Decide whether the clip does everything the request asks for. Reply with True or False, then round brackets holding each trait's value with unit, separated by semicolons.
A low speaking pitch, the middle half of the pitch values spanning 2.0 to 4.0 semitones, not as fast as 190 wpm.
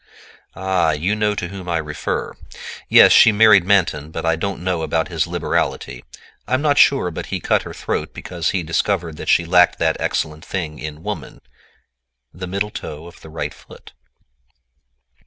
True (85 Hz; 3.5 semitones; 175 wpm)